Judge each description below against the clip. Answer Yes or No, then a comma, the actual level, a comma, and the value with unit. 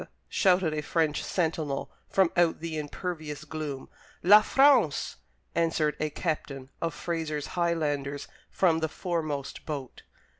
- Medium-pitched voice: Yes, medium, 160 Hz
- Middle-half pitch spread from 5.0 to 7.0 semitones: No, narrow, 2.4 semitones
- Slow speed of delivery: Yes, slow, 125 wpm